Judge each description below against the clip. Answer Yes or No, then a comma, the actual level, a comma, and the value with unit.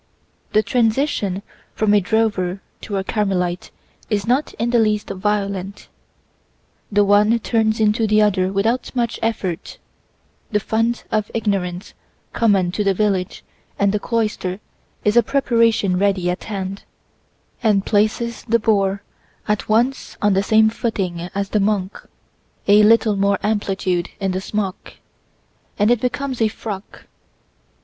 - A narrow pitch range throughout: Yes, narrow, 2.3 semitones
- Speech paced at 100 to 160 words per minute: Yes, average, 140 wpm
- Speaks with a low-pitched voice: No, high, 210 Hz